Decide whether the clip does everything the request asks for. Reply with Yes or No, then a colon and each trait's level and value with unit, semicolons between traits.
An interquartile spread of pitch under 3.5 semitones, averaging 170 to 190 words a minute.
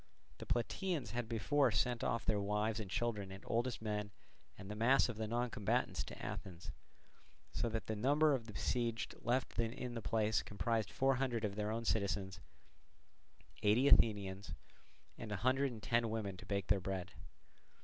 Yes: average, 2.7 semitones; average, 175 wpm